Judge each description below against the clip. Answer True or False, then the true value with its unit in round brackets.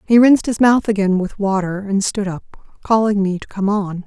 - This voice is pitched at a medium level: False (205 Hz)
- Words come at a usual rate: False (220 wpm)